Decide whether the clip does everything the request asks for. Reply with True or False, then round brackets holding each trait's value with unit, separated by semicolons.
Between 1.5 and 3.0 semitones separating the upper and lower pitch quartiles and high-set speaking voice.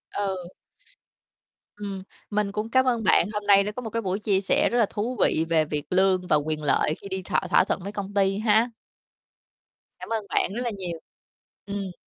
True (2.4 semitones; 200 Hz)